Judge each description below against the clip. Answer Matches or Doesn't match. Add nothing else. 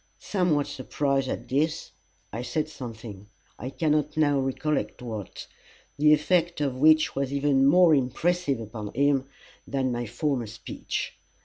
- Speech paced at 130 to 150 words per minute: Matches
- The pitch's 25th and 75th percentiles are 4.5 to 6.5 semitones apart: Doesn't match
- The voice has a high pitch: Doesn't match